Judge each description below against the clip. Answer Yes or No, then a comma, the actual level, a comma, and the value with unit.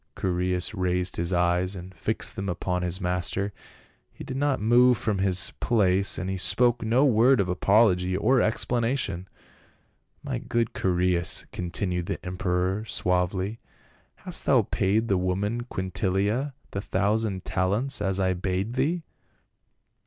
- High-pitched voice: No, very low, 95 Hz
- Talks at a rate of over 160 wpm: No, average, 145 wpm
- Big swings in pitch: No, average, 3.7 semitones